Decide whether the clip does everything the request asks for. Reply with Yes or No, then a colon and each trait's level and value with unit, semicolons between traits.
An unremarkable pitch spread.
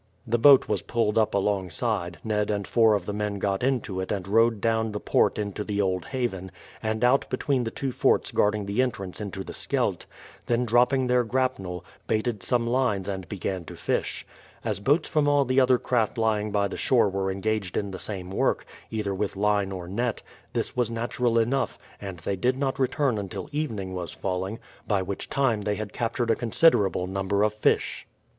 Yes: average, 3.7 semitones